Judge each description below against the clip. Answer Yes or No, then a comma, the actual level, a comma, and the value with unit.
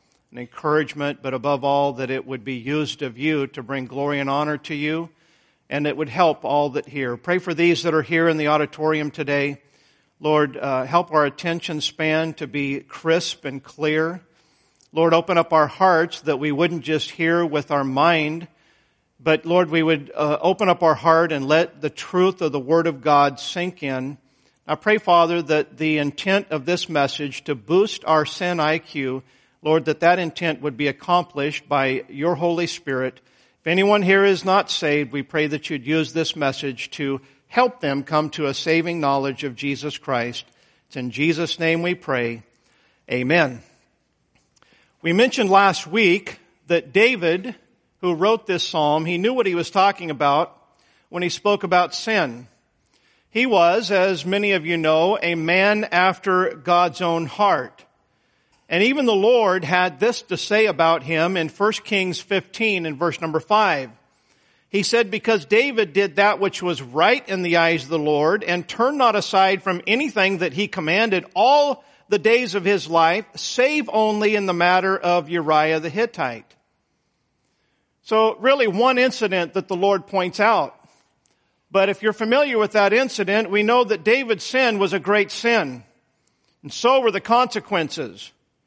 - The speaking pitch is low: No, medium, 170 Hz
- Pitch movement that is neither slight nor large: Yes, average, 4.8 semitones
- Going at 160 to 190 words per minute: Yes, average, 175 wpm